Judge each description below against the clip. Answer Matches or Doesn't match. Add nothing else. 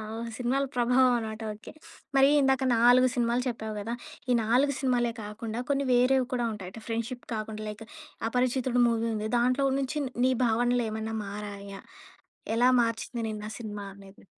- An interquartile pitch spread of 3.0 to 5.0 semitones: Doesn't match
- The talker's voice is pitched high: Matches